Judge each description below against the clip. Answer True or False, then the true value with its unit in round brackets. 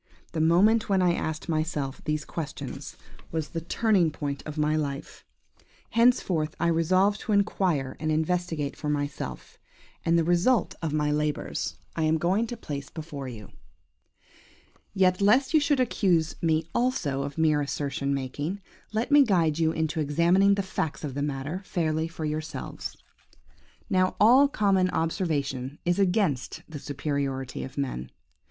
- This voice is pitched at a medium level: True (160 Hz)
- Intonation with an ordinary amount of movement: True (4.3 semitones)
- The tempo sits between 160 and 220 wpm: False (150 wpm)